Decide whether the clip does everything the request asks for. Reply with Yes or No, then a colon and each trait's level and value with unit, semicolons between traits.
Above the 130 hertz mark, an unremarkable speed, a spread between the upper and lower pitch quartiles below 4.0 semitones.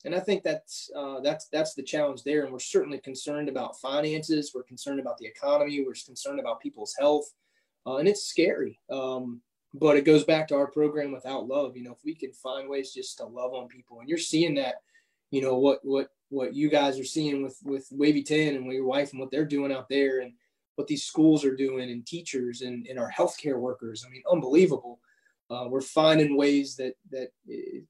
No: medium, 140 Hz; fast, 215 wpm; average, 3.0 semitones